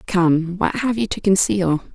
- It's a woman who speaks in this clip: Yes, female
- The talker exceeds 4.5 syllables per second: No, 4.1 syllables/s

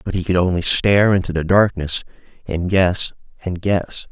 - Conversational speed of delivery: Yes, average, 175 wpm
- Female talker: No, male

